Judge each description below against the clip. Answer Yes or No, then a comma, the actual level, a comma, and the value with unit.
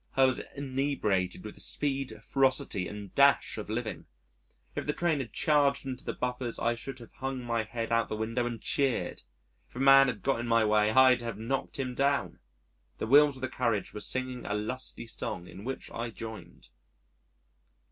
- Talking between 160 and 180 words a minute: No, average, 195 wpm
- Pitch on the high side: No, low, 125 Hz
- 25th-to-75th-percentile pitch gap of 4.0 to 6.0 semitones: No, average, 3.4 semitones